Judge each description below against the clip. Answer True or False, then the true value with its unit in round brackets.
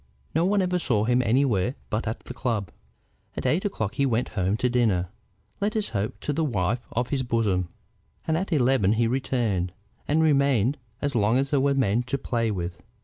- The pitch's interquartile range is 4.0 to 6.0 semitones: True (4.7 semitones)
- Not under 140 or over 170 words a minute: False (200 wpm)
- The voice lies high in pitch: False (125 Hz)